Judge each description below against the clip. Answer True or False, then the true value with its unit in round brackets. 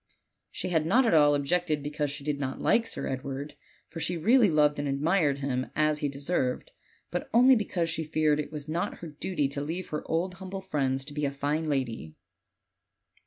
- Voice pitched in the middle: True (150 Hz)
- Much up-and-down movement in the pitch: False (3.5 semitones)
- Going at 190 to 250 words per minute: True (205 wpm)